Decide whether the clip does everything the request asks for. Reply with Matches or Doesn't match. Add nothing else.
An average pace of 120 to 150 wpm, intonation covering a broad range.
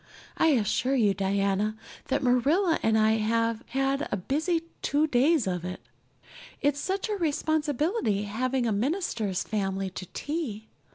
Matches